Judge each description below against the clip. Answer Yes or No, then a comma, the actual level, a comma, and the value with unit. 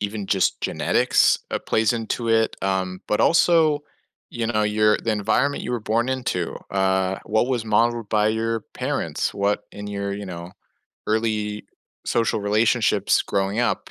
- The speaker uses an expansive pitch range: No, narrow, 2.4 semitones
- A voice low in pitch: Yes, low, 110 Hz